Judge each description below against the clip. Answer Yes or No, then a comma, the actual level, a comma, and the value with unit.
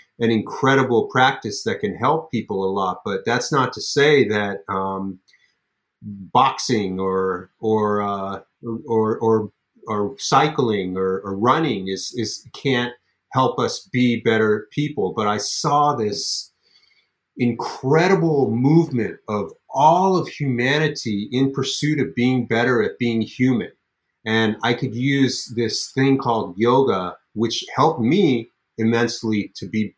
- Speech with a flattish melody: No, average, 4.2 semitones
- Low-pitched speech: Yes, low, 115 Hz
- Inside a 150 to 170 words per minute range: No, slow, 135 wpm